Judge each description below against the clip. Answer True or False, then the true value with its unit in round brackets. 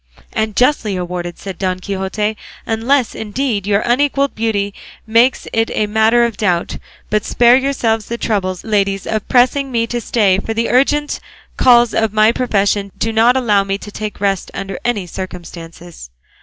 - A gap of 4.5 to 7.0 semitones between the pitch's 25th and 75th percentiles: False (3.4 semitones)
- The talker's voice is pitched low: False (215 Hz)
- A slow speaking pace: False (165 wpm)